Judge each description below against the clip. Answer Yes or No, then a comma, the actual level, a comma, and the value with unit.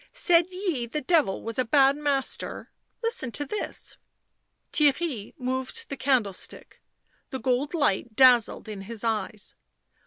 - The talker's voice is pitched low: No, very high, 260 Hz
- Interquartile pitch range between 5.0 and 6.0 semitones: No, average, 4.5 semitones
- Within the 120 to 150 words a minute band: Yes, slow, 135 wpm